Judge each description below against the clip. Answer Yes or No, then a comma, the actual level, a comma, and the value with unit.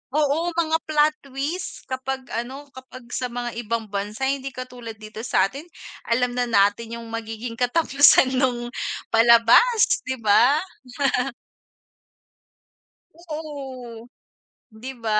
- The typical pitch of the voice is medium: No, very high, 250 Hz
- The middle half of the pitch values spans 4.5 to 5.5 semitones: No, average, 3.3 semitones